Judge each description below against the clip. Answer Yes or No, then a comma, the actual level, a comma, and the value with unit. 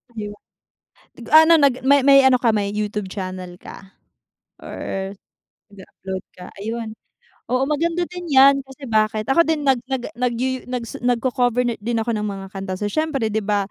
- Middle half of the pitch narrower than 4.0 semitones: No, average, 4.6 semitones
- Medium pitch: No, high, 235 Hz